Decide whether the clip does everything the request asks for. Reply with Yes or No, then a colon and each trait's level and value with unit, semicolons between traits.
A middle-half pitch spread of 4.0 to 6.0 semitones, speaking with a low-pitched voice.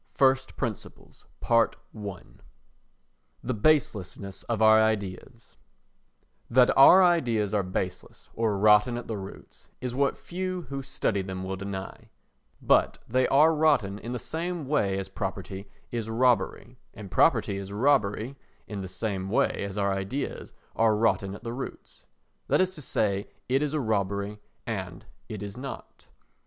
Yes: average, 5.0 semitones; low, 110 Hz